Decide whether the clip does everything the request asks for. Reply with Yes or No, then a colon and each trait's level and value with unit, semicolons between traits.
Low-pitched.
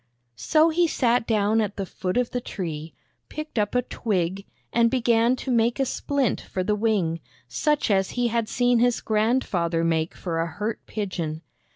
No: high, 220 Hz